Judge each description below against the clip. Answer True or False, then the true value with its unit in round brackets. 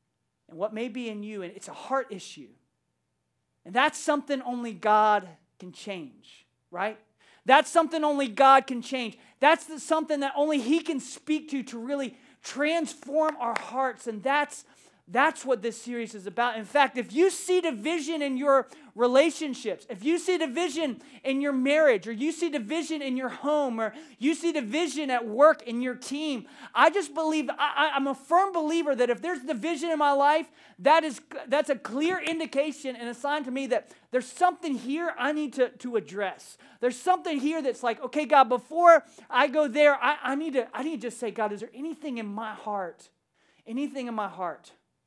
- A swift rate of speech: False (195 wpm)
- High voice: True (275 Hz)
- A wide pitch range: False (4.4 semitones)